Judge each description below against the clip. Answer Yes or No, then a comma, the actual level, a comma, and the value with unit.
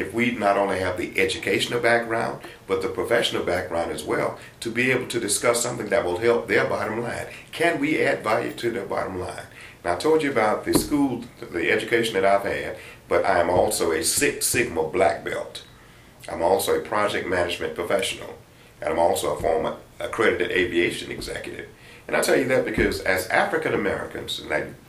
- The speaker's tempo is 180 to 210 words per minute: Yes, average, 190 wpm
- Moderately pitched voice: No, low, 120 Hz